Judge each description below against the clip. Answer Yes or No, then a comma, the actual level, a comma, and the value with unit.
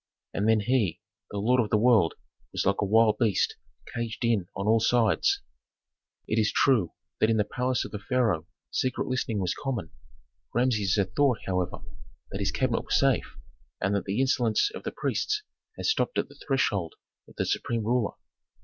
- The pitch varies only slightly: No, average, 3.7 semitones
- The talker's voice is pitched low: Yes, low, 110 Hz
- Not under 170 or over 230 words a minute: Yes, average, 180 wpm